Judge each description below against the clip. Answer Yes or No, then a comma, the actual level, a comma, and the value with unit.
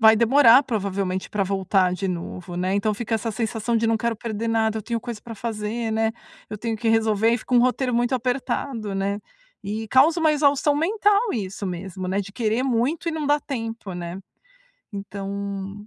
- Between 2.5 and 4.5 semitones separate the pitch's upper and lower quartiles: Yes, average, 3.4 semitones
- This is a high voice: Yes, high, 220 Hz